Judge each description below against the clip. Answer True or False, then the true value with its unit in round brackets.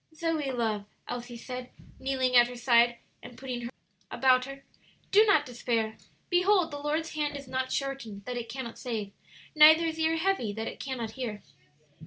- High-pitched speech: True (255 Hz)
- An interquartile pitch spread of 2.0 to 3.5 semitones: False (4.1 semitones)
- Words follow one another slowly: False (180 wpm)